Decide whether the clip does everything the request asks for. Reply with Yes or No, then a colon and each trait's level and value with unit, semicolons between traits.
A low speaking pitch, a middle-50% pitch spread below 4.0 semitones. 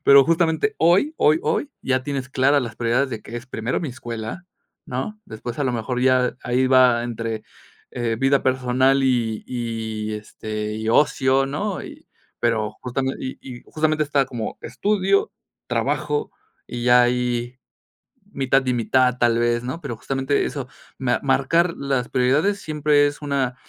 Yes: low, 130 Hz; average, 3.0 semitones